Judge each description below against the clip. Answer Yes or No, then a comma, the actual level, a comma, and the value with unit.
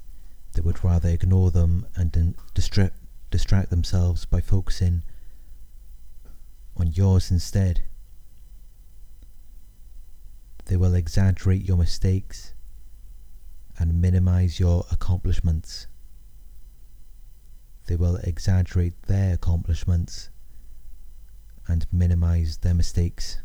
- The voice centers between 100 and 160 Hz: No, very low, 90 Hz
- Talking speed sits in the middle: No, slow, 80 wpm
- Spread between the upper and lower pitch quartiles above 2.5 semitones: No, narrow, 1.7 semitones